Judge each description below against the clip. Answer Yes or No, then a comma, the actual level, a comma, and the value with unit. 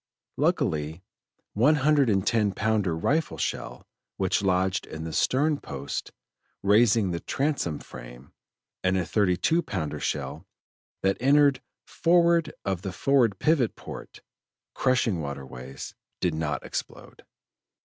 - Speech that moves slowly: Yes, slow, 125 wpm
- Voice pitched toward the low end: Yes, low, 100 Hz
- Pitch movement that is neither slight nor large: No, wide, 8.9 semitones